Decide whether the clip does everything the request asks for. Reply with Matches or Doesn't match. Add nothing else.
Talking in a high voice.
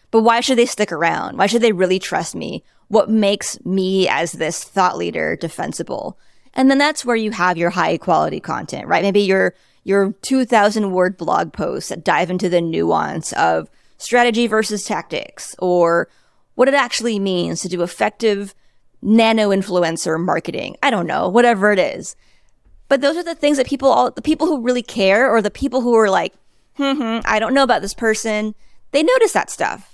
Matches